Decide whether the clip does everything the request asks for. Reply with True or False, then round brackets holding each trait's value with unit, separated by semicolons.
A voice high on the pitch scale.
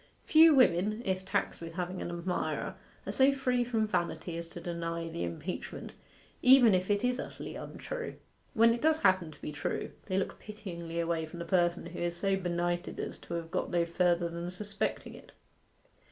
False (180 Hz)